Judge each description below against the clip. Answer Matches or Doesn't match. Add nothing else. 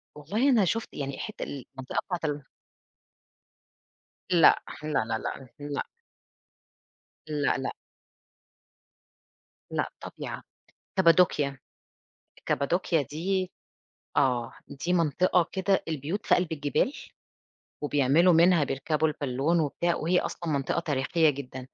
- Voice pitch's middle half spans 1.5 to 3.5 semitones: Doesn't match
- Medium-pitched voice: Matches